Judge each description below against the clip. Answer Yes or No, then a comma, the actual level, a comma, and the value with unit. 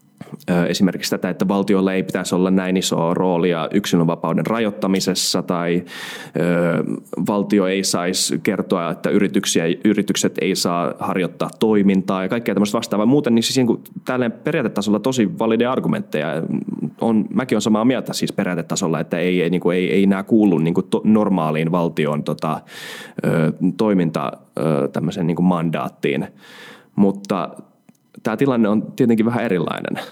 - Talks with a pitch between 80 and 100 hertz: Yes, very low, 95 Hz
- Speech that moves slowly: No, average, 140 wpm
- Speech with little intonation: No, average, 3.3 semitones